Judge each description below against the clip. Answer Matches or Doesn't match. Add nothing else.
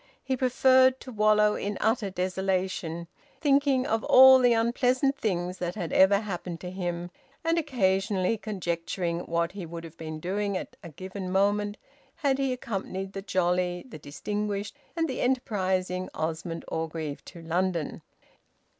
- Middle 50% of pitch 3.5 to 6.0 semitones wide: Matches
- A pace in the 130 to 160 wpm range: Matches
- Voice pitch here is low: Doesn't match